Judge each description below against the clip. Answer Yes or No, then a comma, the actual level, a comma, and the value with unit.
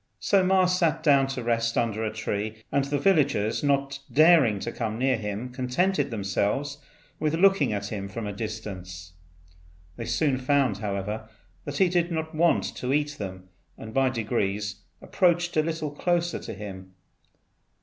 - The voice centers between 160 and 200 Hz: No, low, 130 Hz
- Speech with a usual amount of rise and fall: No, wide, 6.6 semitones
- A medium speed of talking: Yes, average, 160 wpm